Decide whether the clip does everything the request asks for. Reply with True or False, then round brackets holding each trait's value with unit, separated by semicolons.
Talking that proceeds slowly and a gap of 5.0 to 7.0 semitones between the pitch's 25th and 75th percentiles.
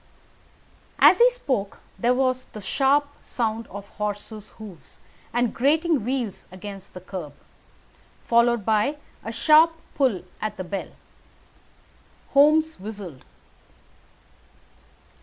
True (105 wpm; 5.4 semitones)